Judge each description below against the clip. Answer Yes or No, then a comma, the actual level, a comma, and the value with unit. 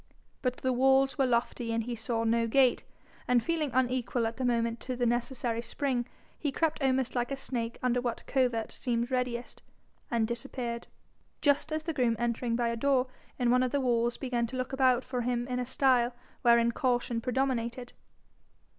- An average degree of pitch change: No, narrow, 1.7 semitones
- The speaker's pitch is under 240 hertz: No, high, 245 Hz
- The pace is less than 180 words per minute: No, average, 185 wpm